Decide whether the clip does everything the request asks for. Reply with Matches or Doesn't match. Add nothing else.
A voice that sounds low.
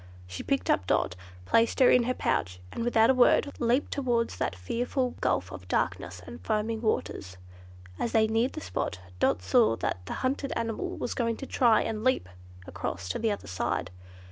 Doesn't match